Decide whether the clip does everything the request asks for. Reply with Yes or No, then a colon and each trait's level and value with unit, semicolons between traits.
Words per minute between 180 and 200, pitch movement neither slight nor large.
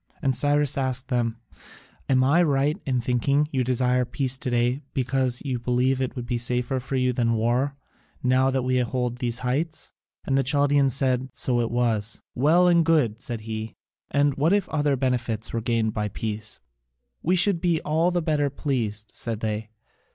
Yes: average, 190 wpm; average, 3.0 semitones